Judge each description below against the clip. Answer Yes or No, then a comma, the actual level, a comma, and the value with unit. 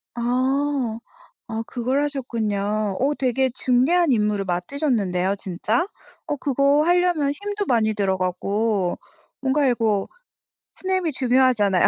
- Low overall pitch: No, high, 245 Hz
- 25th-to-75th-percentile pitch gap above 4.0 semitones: Yes, average, 5.3 semitones